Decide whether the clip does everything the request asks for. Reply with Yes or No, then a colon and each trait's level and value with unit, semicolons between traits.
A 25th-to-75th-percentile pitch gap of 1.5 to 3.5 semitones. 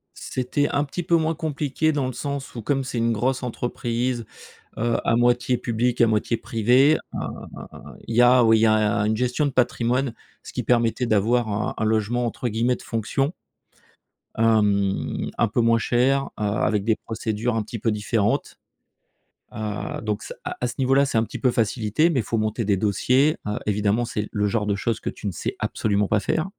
Yes: average, 2.9 semitones